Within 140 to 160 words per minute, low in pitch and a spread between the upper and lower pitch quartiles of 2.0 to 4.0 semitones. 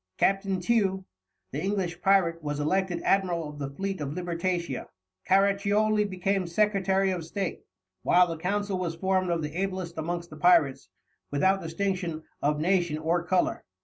No: average, 150 wpm; medium, 180 Hz; average, 2.8 semitones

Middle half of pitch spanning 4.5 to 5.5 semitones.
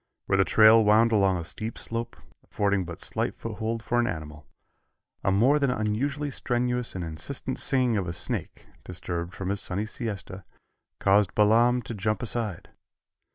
No: average, 3.7 semitones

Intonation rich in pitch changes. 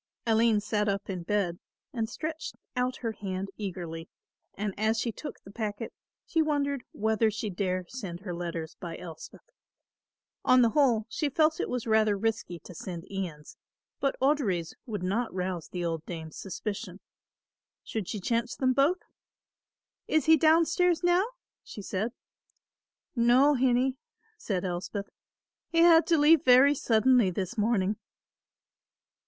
Yes: wide, 5.7 semitones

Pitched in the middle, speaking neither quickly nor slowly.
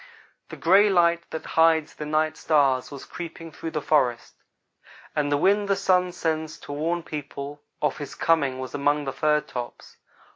Yes: medium, 155 Hz; average, 180 wpm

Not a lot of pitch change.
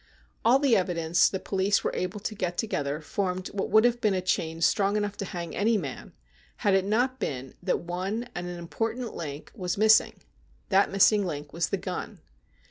No: average, 3.7 semitones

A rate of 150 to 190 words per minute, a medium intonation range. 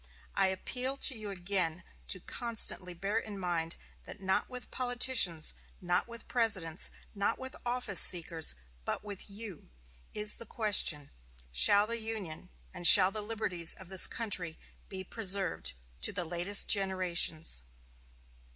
No: average, 140 wpm; average, 4.0 semitones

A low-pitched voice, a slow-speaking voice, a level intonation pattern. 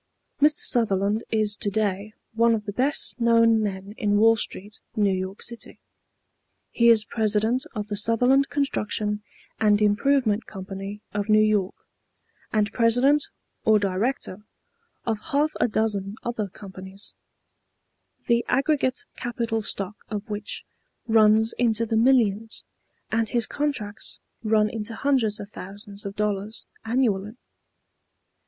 No: high, 215 Hz; slow, 130 wpm; narrow, 2.2 semitones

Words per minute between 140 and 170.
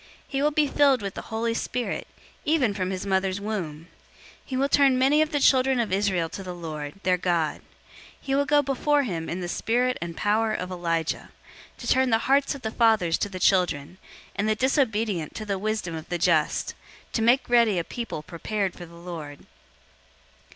No: average, 200 wpm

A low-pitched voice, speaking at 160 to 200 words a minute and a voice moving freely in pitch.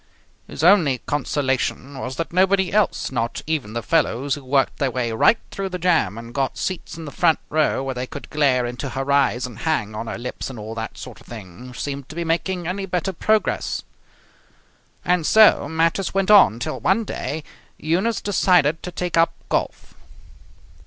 No: medium, 145 Hz; average, 185 wpm; wide, 5.9 semitones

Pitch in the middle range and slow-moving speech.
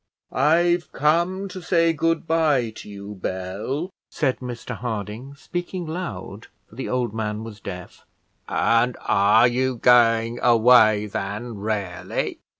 No: low, 120 Hz; slow, 130 wpm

